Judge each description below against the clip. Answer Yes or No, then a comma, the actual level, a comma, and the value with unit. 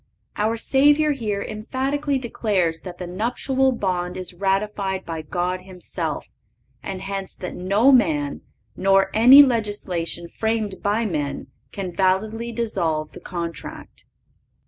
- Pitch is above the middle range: Yes, high, 195 Hz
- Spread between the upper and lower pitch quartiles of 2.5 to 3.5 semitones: No, average, 4.3 semitones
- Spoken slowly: Yes, slow, 125 wpm